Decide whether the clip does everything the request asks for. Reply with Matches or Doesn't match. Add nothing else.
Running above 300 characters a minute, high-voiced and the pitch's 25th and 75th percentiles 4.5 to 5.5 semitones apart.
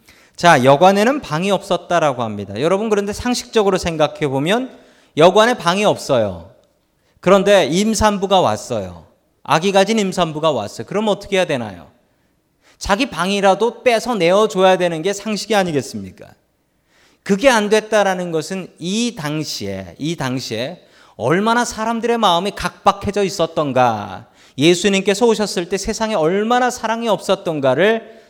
Matches